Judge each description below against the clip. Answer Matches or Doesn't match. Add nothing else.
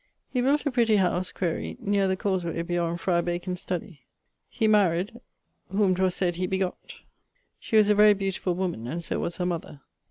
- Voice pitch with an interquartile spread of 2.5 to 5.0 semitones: Matches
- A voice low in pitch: Doesn't match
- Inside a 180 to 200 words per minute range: Matches